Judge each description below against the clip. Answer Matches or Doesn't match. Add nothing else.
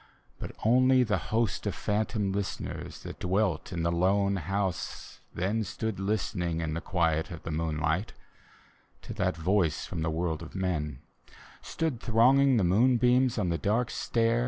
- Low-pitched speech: Matches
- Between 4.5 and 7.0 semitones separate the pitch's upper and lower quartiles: Matches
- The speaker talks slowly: Doesn't match